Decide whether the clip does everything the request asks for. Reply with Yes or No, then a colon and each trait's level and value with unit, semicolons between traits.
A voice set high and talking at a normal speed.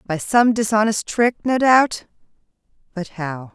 No: high, 215 Hz; slow, 120 wpm